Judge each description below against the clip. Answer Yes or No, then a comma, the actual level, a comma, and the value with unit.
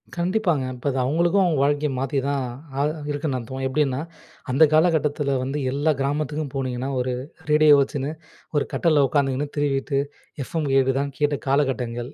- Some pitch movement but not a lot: No, narrow, 2.2 semitones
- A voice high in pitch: No, medium, 140 Hz